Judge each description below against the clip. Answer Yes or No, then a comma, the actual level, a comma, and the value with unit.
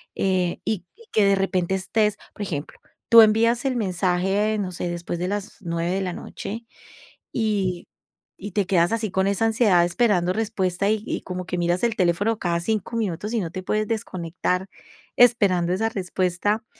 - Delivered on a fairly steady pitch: No, average, 3.3 semitones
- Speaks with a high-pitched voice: Yes, high, 195 Hz